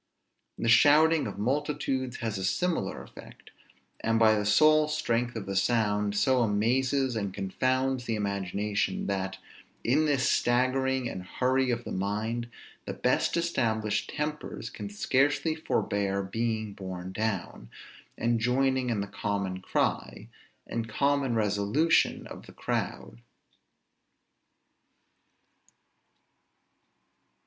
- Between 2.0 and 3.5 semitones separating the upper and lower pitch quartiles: No, average, 4.4 semitones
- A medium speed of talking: No, slow, 115 wpm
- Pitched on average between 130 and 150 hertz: No, low, 115 Hz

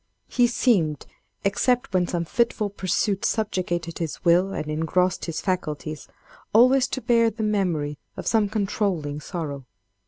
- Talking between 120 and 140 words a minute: Yes, slow, 135 wpm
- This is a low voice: No, medium, 185 Hz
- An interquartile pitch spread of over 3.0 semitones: Yes, average, 5.3 semitones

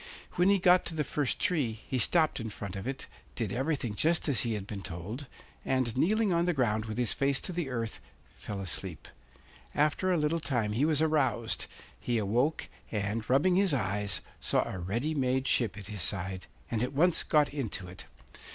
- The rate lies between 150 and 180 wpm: No, average, 195 wpm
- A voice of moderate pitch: No, low, 125 Hz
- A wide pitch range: Yes, wide, 6.5 semitones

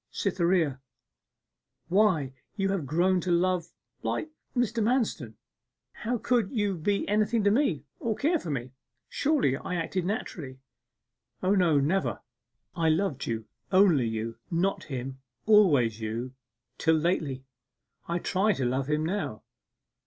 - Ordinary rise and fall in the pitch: No, wide, 6.8 semitones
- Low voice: No, medium, 175 Hz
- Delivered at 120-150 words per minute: Yes, average, 140 wpm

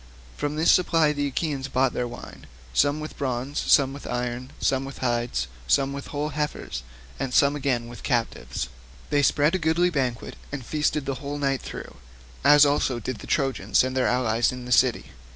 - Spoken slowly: No, average, 190 wpm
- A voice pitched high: No, low, 135 Hz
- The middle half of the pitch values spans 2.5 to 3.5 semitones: Yes, average, 2.9 semitones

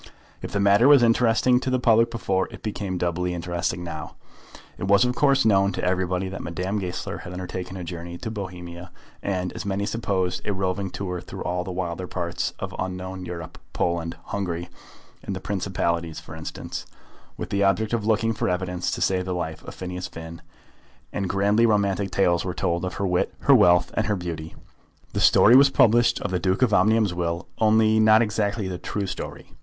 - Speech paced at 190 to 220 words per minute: Yes, average, 195 wpm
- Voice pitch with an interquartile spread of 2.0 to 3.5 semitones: Yes, average, 3.0 semitones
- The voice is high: No, very low, 95 Hz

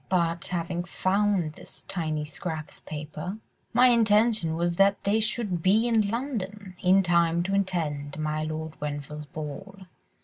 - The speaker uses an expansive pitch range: No, average, 4.4 semitones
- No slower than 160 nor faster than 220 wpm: No, average, 145 wpm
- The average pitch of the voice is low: No, medium, 175 Hz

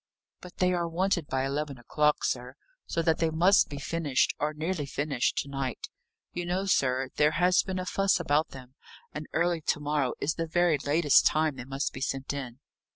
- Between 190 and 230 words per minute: Yes, average, 200 wpm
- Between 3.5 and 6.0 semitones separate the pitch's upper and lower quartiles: Yes, average, 3.9 semitones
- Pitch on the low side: No, medium, 150 Hz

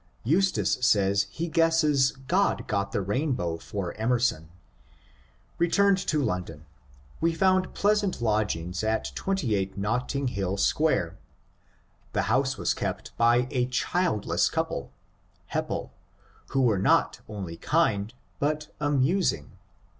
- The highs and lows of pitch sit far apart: Yes, wide, 8.2 semitones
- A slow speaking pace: Yes, slow, 115 wpm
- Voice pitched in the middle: No, low, 125 Hz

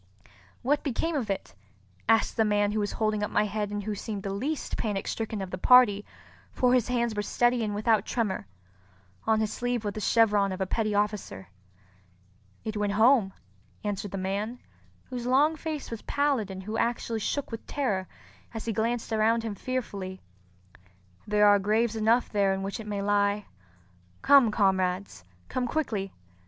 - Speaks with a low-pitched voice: No, high, 215 Hz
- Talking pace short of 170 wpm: No, average, 175 wpm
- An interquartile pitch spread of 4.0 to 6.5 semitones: No, average, 2.7 semitones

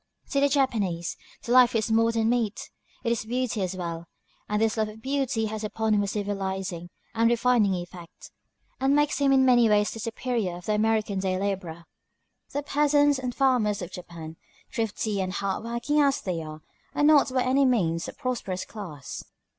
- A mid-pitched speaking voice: No, high, 220 Hz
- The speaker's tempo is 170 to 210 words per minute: Yes, average, 185 wpm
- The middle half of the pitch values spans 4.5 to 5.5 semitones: Yes, average, 4.9 semitones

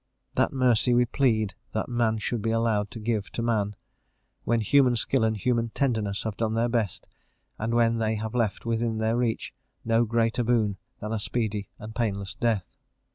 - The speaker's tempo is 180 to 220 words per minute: Yes, average, 185 wpm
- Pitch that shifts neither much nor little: No, narrow, 1.7 semitones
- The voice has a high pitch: No, low, 115 Hz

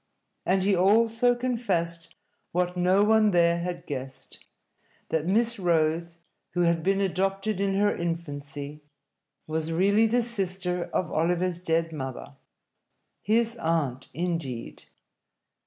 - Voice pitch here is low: No, medium, 180 Hz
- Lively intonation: No, average, 3.4 semitones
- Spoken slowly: Yes, slow, 120 wpm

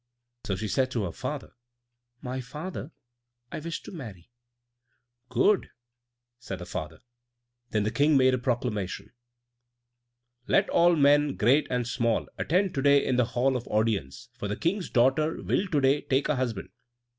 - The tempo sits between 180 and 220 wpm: No, average, 160 wpm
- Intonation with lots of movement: No, average, 5.0 semitones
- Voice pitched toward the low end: Yes, low, 130 Hz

